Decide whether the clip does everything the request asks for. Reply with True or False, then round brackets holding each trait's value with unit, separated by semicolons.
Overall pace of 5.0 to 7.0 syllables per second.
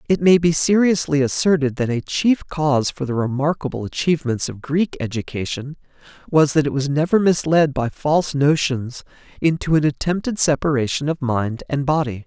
True (5.2 syllables/s)